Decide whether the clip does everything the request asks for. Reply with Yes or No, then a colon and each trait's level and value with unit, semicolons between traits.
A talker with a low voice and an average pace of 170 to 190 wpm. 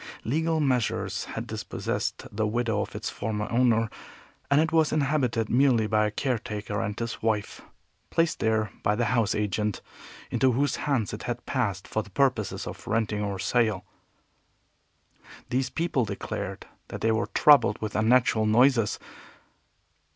No: low, 115 Hz; average, 150 wpm